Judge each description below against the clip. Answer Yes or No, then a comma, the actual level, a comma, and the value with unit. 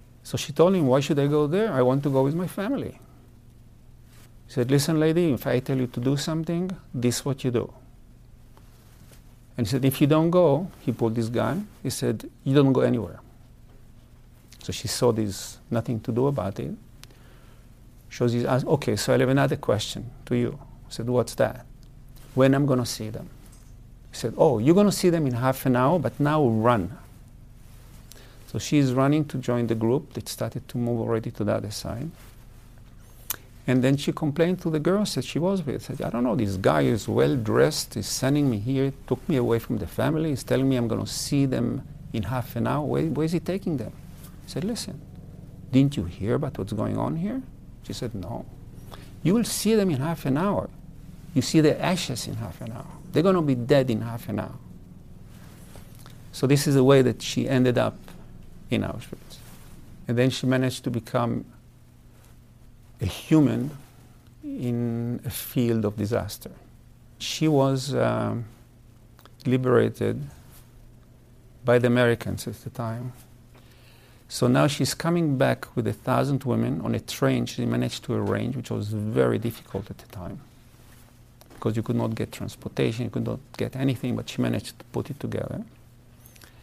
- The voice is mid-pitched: No, low, 125 Hz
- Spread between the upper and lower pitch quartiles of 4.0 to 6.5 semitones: No, average, 2.9 semitones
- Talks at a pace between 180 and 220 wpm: Yes, average, 190 wpm